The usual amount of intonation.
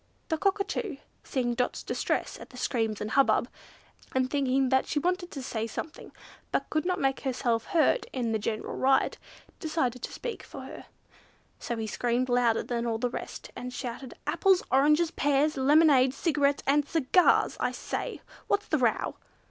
Yes: average, 4.1 semitones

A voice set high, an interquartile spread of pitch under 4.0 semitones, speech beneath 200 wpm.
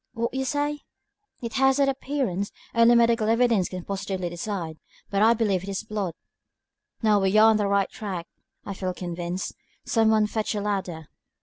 Yes: high, 210 Hz; average, 3.5 semitones; average, 180 wpm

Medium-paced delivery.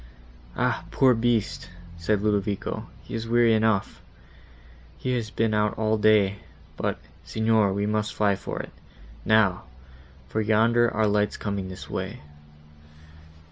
No: slow, 130 wpm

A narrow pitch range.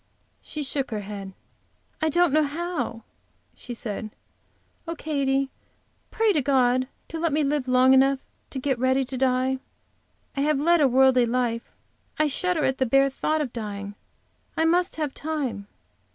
No: average, 3.4 semitones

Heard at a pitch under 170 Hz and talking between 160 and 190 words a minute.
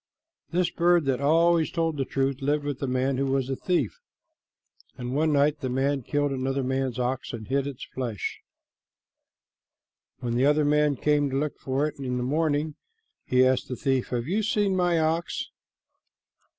Yes: medium, 140 Hz; average, 175 wpm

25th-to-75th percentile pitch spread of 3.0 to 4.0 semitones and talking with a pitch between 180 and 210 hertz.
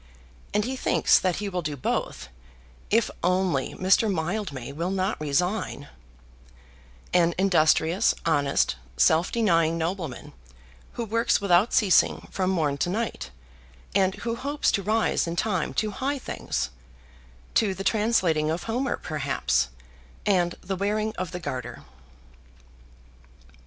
No: average, 4.8 semitones; medium, 185 Hz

